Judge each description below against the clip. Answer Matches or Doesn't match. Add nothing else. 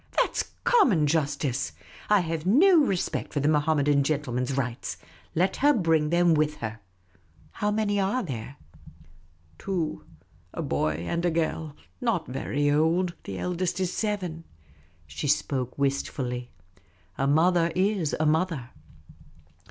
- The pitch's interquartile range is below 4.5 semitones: Doesn't match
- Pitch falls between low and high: Matches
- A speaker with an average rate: Matches